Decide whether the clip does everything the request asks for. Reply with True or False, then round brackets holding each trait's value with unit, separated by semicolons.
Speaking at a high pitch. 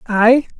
True (235 Hz)